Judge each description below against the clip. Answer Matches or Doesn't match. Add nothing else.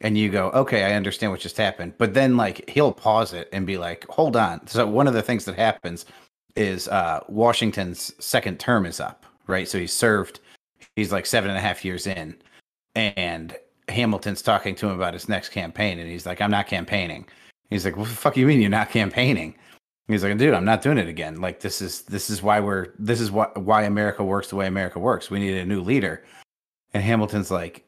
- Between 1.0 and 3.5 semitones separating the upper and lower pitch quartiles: Matches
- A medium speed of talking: Doesn't match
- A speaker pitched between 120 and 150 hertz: Doesn't match